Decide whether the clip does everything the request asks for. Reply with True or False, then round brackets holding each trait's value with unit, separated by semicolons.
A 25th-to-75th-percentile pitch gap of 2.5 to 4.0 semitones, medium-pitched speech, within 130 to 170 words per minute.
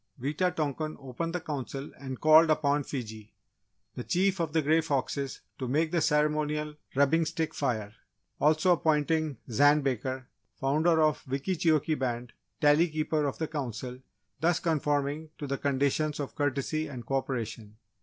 True (2.8 semitones; 150 Hz; 150 wpm)